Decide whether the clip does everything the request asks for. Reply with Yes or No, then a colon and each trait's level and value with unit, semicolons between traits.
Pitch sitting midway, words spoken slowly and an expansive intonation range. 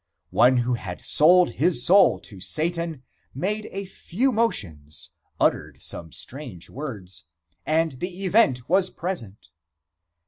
Yes: medium, 155 Hz; slow, 125 wpm; wide, 8.3 semitones